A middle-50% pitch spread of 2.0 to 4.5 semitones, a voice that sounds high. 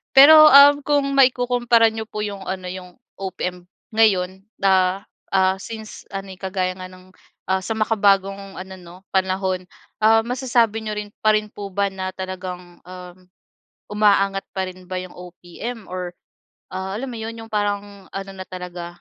Yes: average, 2.9 semitones; high, 195 Hz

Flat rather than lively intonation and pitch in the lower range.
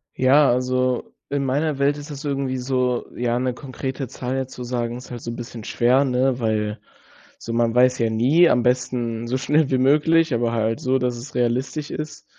Yes: narrow, 2.2 semitones; low, 125 Hz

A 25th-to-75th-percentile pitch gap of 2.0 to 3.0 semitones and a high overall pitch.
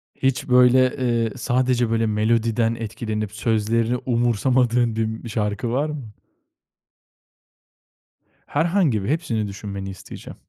No: narrow, 2.5 semitones; low, 115 Hz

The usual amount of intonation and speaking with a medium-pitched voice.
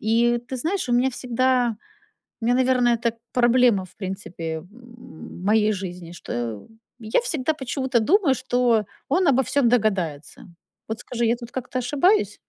No: average, 3.3 semitones; high, 240 Hz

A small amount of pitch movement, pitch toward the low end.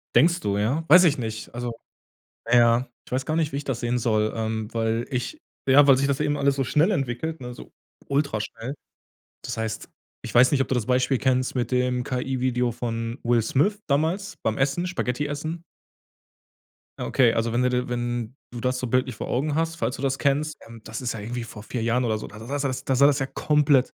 No: average, 3.1 semitones; low, 125 Hz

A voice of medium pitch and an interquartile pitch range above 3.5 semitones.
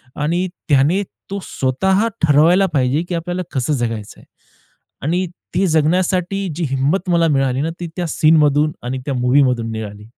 Yes: medium, 150 Hz; average, 5.0 semitones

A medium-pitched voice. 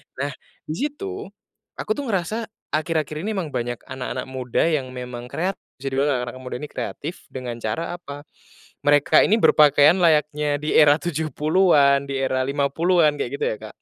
Yes: medium, 150 Hz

